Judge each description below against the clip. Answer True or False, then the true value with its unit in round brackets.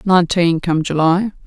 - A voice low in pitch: False (175 Hz)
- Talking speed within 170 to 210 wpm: False (125 wpm)